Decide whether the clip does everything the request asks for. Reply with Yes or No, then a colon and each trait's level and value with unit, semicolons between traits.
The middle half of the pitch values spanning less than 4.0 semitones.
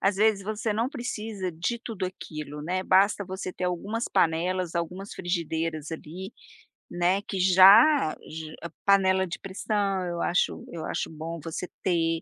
Yes: average, 3.1 semitones